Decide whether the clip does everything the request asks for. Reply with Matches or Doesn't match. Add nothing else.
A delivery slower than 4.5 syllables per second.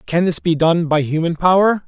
Doesn't match